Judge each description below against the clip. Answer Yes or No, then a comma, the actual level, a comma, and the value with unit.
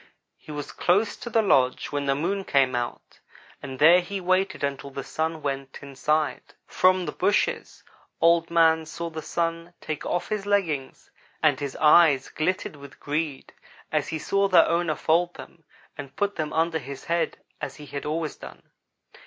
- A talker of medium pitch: Yes, medium, 160 Hz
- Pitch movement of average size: Yes, average, 3.7 semitones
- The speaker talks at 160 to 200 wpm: Yes, average, 175 wpm